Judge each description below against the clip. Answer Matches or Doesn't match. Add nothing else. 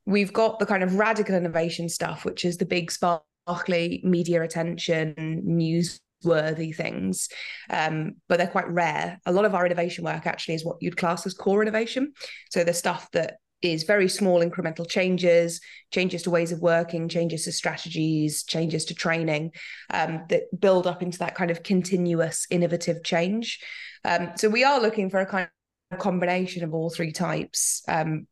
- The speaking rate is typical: Matches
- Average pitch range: Doesn't match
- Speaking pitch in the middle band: Matches